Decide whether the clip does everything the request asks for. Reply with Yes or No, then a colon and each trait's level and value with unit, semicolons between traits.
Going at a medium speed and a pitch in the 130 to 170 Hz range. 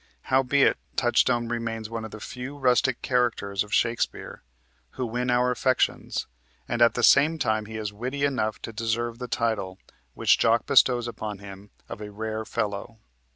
No: average, 165 wpm; low, 115 Hz